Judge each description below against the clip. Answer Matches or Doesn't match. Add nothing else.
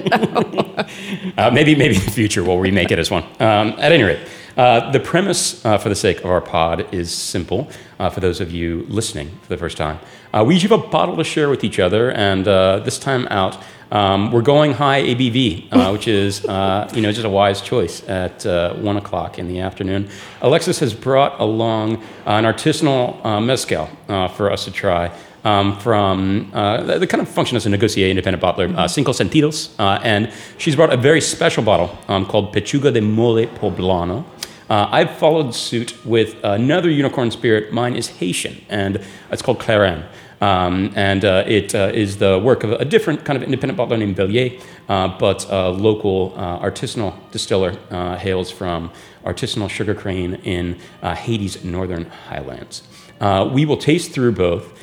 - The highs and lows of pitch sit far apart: Doesn't match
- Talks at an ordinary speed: Matches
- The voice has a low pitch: Matches